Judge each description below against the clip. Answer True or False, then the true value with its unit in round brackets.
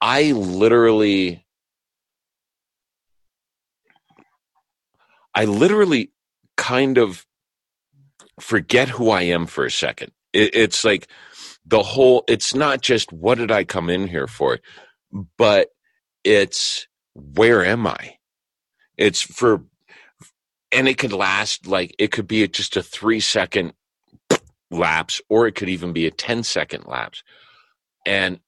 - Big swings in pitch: True (6.2 semitones)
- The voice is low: True (110 Hz)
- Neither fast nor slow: False (120 wpm)